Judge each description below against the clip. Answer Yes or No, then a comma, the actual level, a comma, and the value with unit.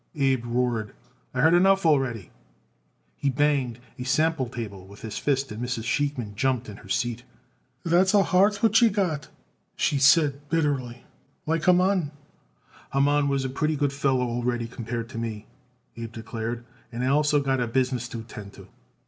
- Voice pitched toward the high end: No, low, 130 Hz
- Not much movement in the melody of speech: No, average, 4.1 semitones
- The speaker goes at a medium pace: Yes, average, 165 wpm